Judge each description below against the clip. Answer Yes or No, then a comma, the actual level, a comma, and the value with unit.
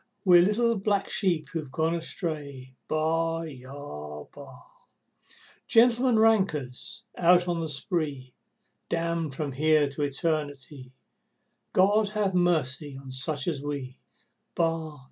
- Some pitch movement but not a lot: Yes, average, 4.1 semitones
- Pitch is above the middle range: No, medium, 155 Hz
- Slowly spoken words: Yes, slow, 115 wpm